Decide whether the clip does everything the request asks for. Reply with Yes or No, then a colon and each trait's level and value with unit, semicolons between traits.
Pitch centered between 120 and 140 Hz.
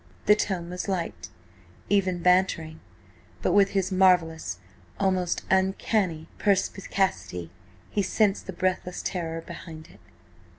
No: medium, 185 Hz